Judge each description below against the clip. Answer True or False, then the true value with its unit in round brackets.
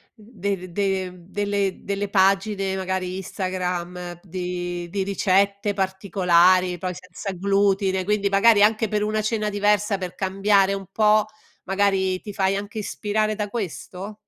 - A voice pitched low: False (195 Hz)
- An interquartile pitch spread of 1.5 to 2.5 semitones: True (1.8 semitones)